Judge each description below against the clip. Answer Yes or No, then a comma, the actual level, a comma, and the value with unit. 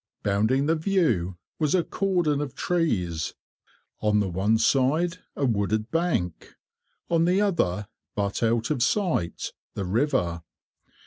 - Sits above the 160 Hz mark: No, low, 125 Hz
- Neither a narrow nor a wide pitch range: No, wide, 8.6 semitones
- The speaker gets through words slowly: Yes, slow, 130 wpm